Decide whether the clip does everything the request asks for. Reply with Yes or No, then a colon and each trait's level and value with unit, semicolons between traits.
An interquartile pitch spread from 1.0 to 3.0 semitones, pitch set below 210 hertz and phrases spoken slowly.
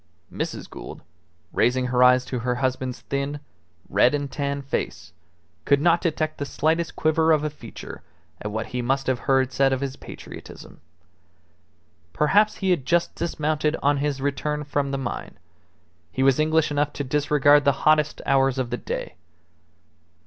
No: narrow, 2.6 semitones; medium, 140 Hz; average, 165 wpm